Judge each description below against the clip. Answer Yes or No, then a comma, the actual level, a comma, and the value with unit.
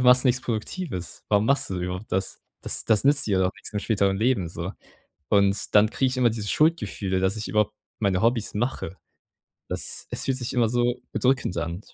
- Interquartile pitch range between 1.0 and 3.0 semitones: No, average, 4.5 semitones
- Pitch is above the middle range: No, low, 105 Hz